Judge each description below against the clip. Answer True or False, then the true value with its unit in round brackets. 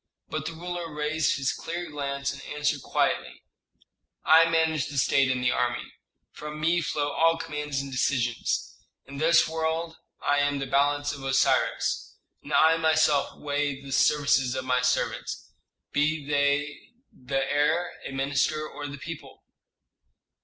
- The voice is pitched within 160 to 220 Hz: False (145 Hz)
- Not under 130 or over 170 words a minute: True (150 wpm)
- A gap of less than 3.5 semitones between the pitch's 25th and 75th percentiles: True (2.4 semitones)